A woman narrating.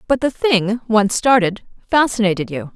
Yes: female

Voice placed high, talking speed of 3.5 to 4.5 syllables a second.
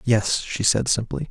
No: low, 120 Hz; 4.1 syllables/s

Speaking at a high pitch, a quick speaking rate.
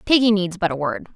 Yes: high, 195 Hz; fast, 260 wpm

